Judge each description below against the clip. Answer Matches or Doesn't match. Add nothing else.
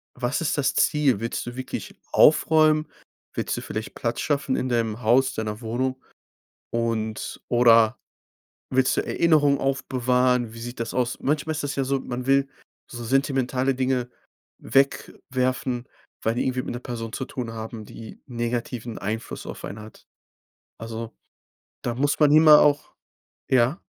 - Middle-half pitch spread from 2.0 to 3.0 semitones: Matches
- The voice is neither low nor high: Doesn't match